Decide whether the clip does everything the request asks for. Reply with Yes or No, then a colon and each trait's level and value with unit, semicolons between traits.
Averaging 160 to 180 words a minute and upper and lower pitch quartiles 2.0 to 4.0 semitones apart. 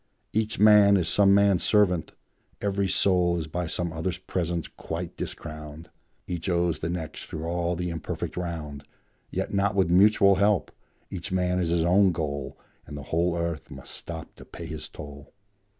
Yes: average, 170 wpm; average, 2.9 semitones